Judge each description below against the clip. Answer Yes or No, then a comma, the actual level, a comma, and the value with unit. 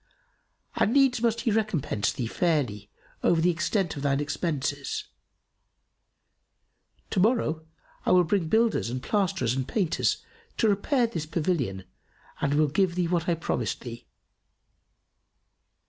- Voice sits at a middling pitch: Yes, medium, 165 Hz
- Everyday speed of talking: No, slow, 130 wpm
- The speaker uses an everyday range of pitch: No, wide, 6.3 semitones